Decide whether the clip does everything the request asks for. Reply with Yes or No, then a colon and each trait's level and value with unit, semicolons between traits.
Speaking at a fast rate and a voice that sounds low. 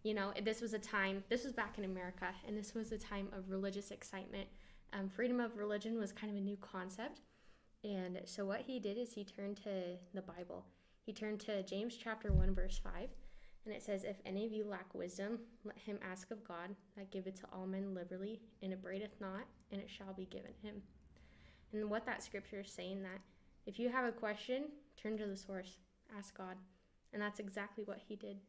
No: fast, 215 wpm; high, 200 Hz